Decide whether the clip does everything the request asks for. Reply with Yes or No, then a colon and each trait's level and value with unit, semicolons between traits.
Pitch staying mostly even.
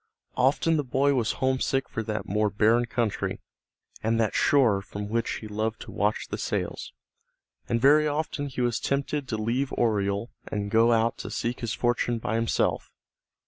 No: average, 3.3 semitones